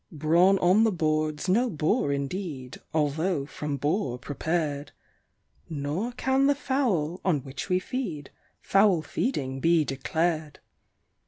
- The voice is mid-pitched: Yes, medium, 160 Hz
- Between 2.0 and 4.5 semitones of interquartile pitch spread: No, average, 4.9 semitones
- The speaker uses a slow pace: Yes, slow, 120 wpm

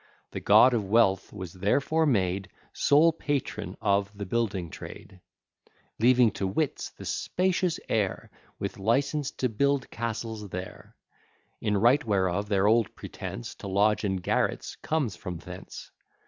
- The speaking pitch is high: No, low, 110 Hz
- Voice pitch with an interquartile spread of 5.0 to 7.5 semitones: Yes, average, 5.3 semitones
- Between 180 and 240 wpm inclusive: No, average, 140 wpm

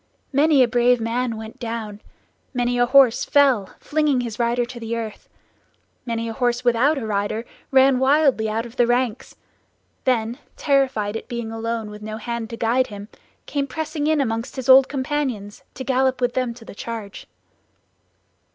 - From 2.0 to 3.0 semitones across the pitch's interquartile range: Yes, average, 2.7 semitones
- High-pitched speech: Yes, high, 240 Hz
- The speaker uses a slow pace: No, average, 170 wpm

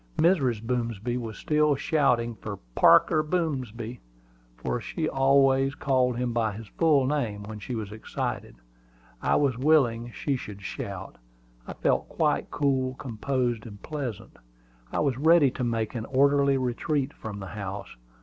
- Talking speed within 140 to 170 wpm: Yes, average, 150 wpm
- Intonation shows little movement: No, average, 3.7 semitones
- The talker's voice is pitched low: Yes, low, 125 Hz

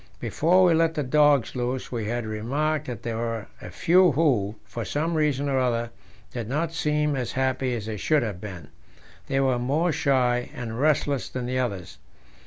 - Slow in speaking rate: No, average, 190 wpm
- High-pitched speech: No, low, 130 Hz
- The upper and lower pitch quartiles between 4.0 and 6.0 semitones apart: Yes, average, 4.4 semitones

